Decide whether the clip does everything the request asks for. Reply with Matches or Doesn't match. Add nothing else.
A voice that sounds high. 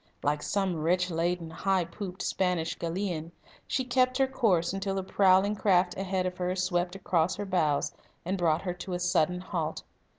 Doesn't match